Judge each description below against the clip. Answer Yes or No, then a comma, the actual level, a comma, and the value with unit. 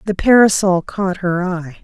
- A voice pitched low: No, medium, 185 Hz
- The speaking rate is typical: Yes, average, 165 wpm